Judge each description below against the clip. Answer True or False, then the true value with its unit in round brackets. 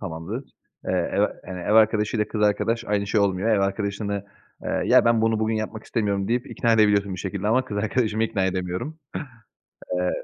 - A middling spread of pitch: False (2.3 semitones)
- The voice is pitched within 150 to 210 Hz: False (105 Hz)